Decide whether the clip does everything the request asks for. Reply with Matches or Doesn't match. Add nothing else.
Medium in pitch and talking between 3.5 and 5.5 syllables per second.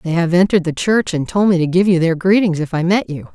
Doesn't match